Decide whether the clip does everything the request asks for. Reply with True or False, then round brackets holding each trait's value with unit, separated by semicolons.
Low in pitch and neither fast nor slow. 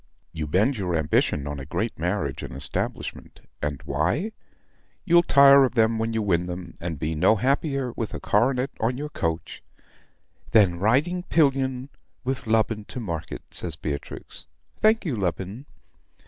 True (110 Hz; 160 wpm)